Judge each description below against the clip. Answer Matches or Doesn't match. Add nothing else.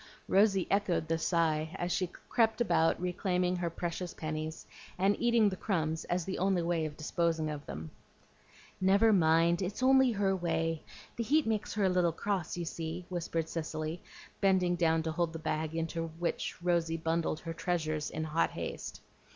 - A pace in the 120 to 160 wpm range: Doesn't match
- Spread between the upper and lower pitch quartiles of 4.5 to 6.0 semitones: Doesn't match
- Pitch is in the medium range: Matches